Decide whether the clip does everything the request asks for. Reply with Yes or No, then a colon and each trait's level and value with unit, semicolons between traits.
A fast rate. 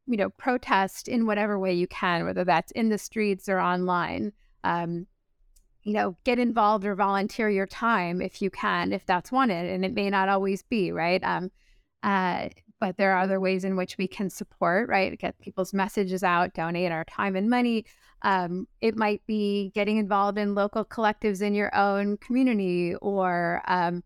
No: average, 185 wpm